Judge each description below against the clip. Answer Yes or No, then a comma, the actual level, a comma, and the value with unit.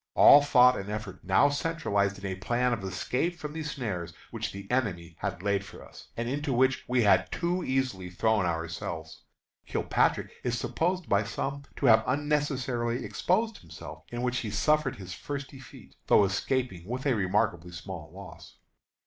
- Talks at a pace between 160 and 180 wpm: Yes, average, 170 wpm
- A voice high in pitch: No, low, 115 Hz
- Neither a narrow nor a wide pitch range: No, wide, 6.4 semitones